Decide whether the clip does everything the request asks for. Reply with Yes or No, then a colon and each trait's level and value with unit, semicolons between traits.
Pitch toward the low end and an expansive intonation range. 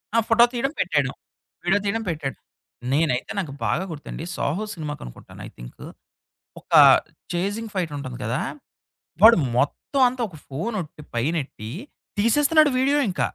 No: medium, 175 Hz; wide, 8.2 semitones